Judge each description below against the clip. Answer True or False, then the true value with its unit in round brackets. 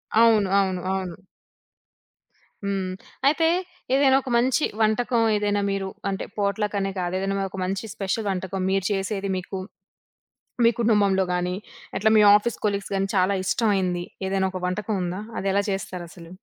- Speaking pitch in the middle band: False (195 Hz)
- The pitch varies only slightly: True (1.9 semitones)